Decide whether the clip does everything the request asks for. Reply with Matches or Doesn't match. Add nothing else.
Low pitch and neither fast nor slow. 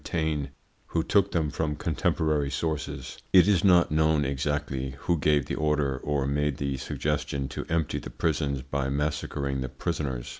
Matches